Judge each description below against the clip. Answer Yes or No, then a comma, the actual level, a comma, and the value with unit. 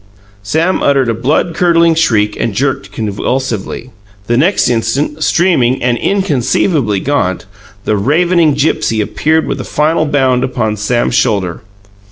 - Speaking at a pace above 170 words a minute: No, slow, 135 wpm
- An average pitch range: No, wide, 5.9 semitones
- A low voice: Yes, low, 130 Hz